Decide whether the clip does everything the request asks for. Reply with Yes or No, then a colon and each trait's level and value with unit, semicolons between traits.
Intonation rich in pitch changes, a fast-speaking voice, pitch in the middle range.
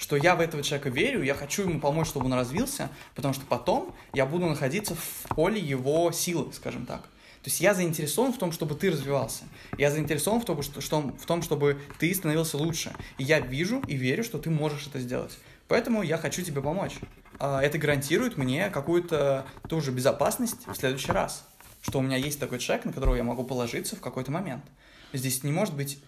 No: average, 3.8 semitones; fast, 205 wpm; medium, 145 Hz